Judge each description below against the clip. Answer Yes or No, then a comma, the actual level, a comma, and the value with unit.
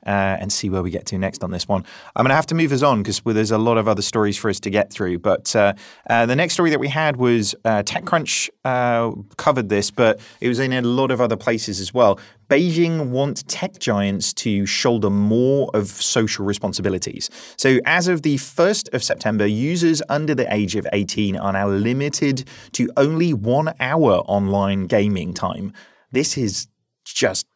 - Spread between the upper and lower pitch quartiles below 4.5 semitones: No, average, 5.3 semitones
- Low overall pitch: Yes, low, 115 Hz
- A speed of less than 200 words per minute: No, fast, 205 wpm